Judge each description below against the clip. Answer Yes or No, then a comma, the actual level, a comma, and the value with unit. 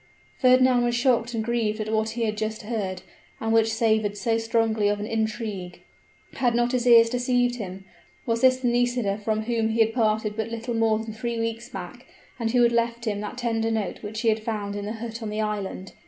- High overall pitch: Yes, high, 225 Hz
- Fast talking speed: Yes, fast, 220 wpm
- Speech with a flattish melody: Yes, narrow, 1.7 semitones